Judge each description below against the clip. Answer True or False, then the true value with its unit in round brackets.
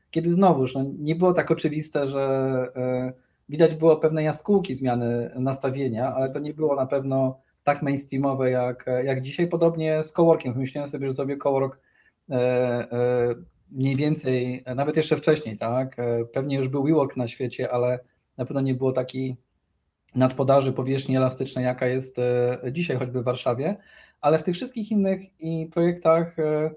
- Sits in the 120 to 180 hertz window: True (135 Hz)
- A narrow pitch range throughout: False (3.5 semitones)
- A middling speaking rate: True (145 wpm)